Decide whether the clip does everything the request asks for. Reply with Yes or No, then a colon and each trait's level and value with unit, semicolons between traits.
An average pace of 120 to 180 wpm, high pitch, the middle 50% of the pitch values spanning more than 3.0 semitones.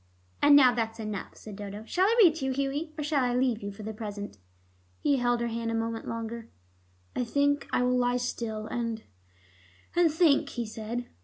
No: fast, 205 wpm; high, 240 Hz; average, 3.9 semitones